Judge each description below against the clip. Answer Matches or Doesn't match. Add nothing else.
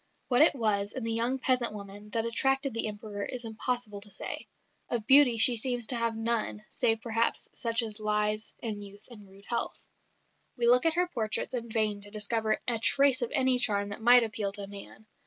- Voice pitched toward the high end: Matches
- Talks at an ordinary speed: Doesn't match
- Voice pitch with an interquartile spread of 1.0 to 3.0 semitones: Matches